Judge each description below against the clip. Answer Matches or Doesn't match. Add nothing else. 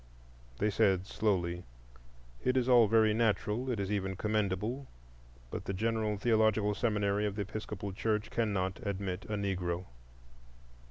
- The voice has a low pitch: Matches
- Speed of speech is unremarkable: Doesn't match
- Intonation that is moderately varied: Doesn't match